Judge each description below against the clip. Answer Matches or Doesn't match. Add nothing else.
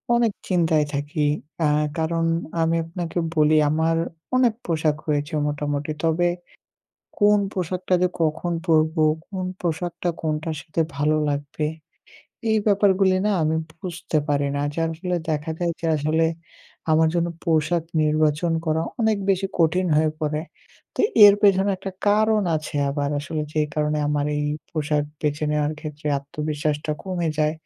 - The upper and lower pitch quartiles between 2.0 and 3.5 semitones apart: Matches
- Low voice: Doesn't match